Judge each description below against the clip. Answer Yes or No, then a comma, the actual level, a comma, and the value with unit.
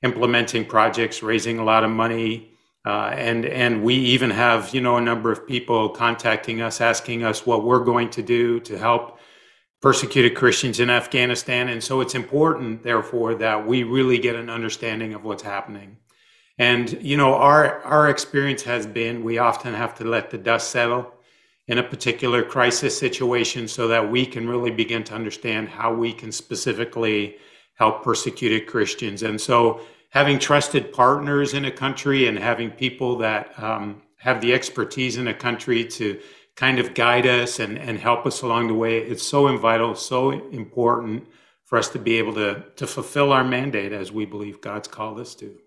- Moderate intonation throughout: No, narrow, 1.7 semitones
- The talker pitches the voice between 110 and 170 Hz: Yes, low, 120 Hz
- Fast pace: No, average, 180 wpm